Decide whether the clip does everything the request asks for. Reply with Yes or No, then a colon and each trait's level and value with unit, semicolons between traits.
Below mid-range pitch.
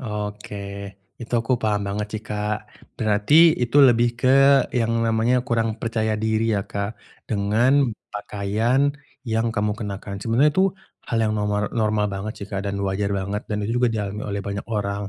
Yes: low, 105 Hz